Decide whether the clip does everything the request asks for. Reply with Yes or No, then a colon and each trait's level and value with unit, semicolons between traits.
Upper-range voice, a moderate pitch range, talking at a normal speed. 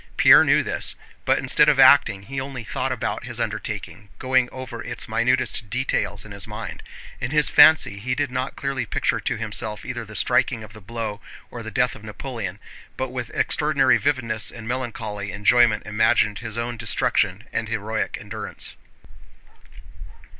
No: low, 115 Hz; average, 3.2 semitones; average, 165 wpm